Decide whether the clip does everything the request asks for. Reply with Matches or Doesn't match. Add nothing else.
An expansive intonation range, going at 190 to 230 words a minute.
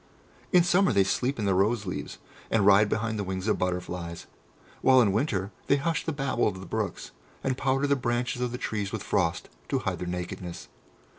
Matches